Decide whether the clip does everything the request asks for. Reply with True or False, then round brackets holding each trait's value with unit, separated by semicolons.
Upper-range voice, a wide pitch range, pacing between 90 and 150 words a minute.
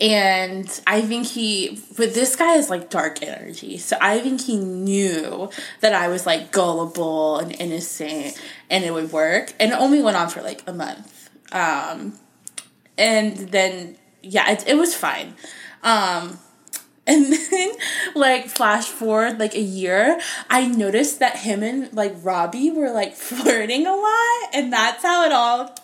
False (215 Hz; 5.7 semitones; 165 wpm)